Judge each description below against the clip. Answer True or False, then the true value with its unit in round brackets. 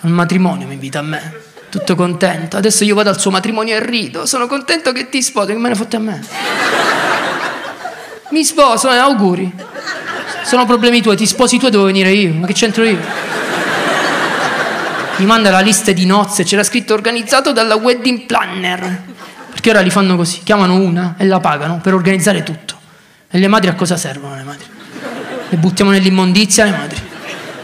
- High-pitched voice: True (200 Hz)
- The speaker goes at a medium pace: False (180 wpm)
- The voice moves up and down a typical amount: True (3.9 semitones)